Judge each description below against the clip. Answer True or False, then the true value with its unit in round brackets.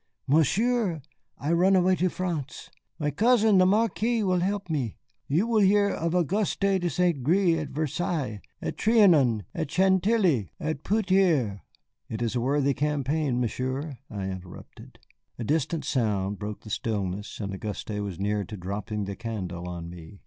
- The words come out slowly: False (165 wpm)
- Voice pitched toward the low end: False (150 Hz)